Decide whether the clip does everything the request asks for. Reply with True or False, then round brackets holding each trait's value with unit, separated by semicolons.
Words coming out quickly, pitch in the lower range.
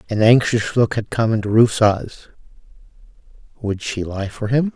False (150 wpm; 115 Hz)